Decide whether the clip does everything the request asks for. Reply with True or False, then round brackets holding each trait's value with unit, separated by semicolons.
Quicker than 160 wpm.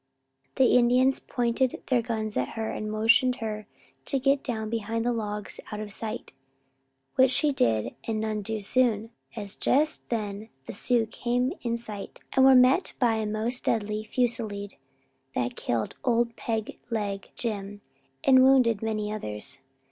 False (155 wpm)